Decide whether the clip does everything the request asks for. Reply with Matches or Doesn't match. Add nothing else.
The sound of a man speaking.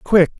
Matches